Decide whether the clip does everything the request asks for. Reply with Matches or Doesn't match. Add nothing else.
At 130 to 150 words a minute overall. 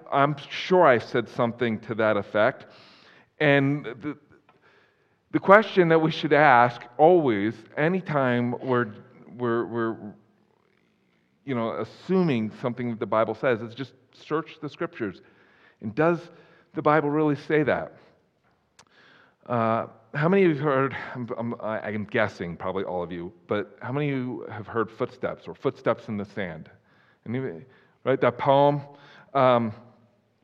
Matches